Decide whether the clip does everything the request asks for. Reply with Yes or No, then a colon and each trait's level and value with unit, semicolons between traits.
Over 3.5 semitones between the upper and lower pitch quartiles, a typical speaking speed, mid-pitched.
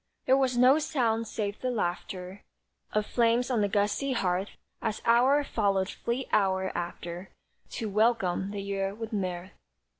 No: average, 3.9 semitones; average, 150 wpm; high, 210 Hz